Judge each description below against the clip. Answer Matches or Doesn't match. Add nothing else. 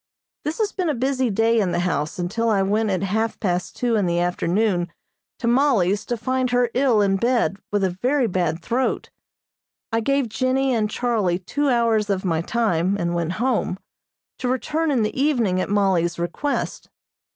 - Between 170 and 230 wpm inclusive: Matches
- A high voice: Matches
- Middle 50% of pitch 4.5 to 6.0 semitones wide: Matches